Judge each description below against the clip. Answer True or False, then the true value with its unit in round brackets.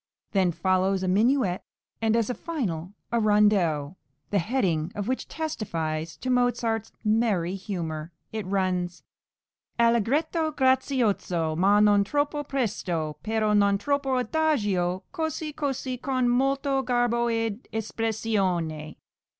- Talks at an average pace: False (120 wpm)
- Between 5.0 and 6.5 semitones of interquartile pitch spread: True (5.6 semitones)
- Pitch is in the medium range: False (215 Hz)